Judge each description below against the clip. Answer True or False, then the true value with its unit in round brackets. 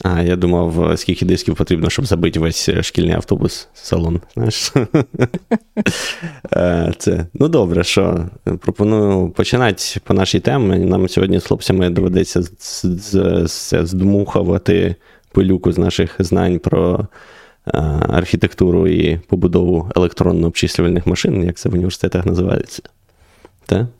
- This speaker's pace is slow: True (100 wpm)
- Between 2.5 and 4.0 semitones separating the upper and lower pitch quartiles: True (2.9 semitones)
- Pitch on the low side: True (90 Hz)